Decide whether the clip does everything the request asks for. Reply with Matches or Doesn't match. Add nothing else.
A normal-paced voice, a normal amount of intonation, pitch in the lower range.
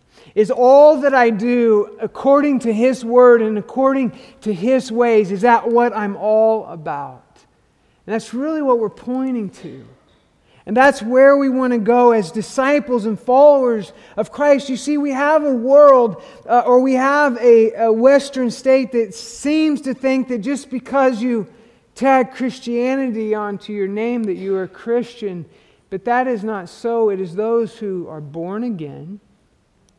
Doesn't match